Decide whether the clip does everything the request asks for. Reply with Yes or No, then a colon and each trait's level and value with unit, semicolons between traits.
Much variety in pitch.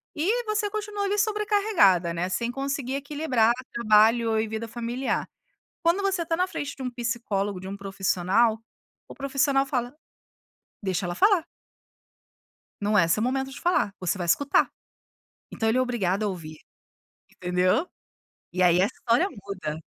Yes: wide, 6.9 semitones